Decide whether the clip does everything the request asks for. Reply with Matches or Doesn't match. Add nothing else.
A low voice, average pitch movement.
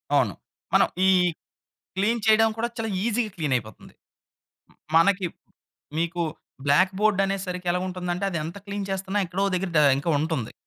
Doesn't match